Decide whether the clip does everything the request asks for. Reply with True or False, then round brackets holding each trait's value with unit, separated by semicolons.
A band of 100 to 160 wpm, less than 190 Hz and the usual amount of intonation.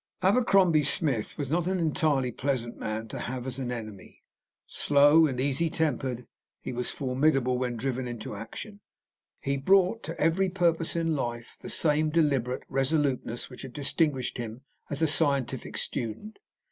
True (150 wpm; 140 Hz; 4.5 semitones)